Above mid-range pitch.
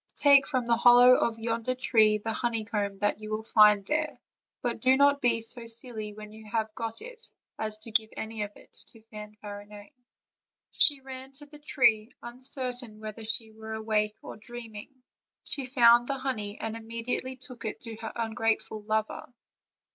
Yes: high, 225 Hz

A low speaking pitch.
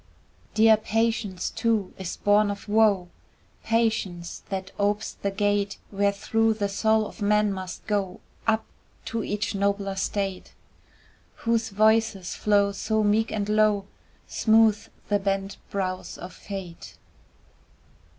No: high, 205 Hz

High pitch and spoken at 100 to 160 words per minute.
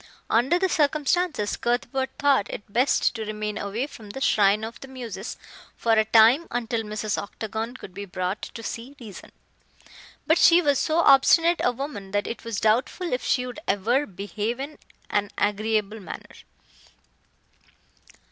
Yes: high, 230 Hz; average, 155 wpm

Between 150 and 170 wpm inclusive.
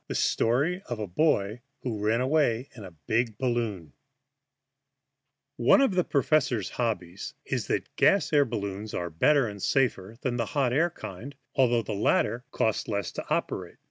Yes: average, 165 wpm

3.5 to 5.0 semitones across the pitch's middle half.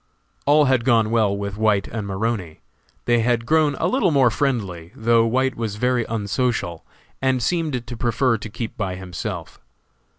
Yes: average, 3.9 semitones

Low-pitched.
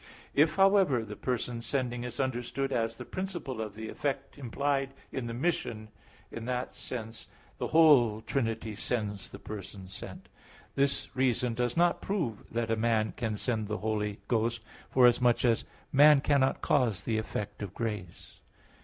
Yes: low, 120 Hz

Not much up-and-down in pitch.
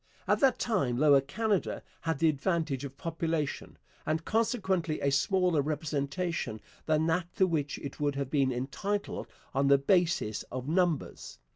No: average, 4.4 semitones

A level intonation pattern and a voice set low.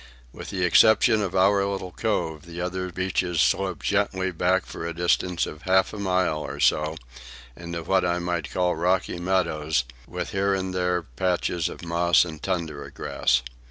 Yes: narrow, 2.0 semitones; very low, 90 Hz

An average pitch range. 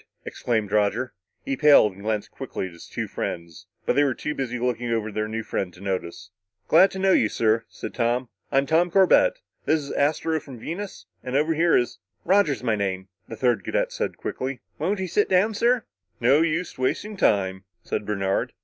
No: wide, 7.5 semitones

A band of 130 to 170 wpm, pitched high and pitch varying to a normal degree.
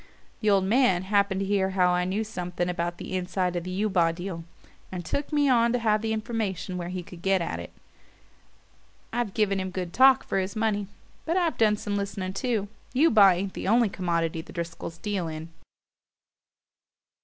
No: average, 185 wpm; high, 195 Hz; average, 3.3 semitones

